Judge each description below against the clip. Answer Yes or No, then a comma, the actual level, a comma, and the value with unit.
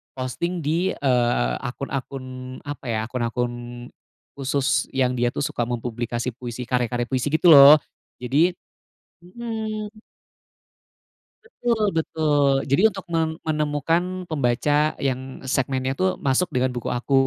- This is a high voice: No, low, 135 Hz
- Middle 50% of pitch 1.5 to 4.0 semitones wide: No, average, 4.4 semitones